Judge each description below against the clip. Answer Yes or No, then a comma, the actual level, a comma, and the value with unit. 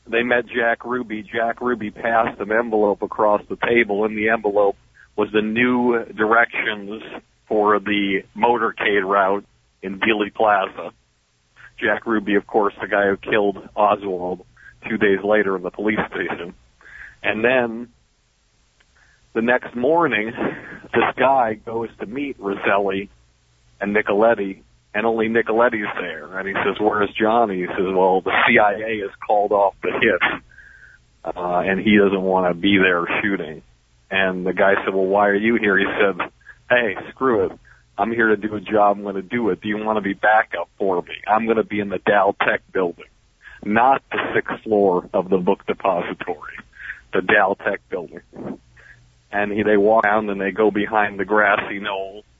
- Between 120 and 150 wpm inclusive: No, average, 170 wpm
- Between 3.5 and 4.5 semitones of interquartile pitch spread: No, narrow, 2.4 semitones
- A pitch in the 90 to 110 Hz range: Yes, low, 105 Hz